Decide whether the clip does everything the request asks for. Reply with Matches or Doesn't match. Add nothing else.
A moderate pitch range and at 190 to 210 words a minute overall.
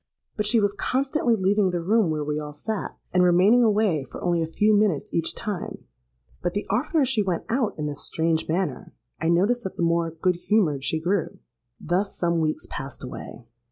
Matches